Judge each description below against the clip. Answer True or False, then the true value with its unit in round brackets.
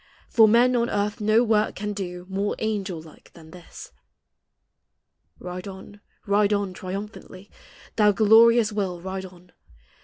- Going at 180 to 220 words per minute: False (140 wpm)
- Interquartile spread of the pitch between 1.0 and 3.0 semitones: True (2.6 semitones)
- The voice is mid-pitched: False (205 Hz)